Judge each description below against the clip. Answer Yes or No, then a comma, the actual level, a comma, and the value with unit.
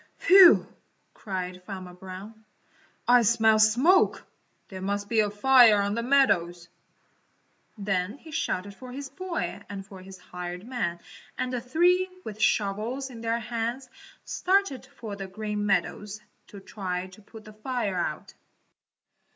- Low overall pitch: No, high, 215 Hz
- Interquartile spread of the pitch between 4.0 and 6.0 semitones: Yes, average, 4.5 semitones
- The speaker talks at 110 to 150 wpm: Yes, average, 145 wpm